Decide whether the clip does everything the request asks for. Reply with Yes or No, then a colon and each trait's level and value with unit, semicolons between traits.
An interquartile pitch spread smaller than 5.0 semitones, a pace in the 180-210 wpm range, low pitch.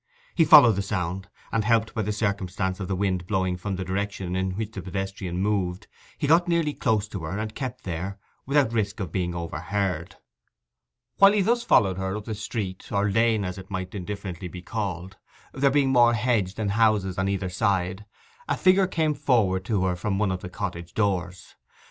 Yes: average, 3.3 semitones; average, 195 wpm; low, 100 Hz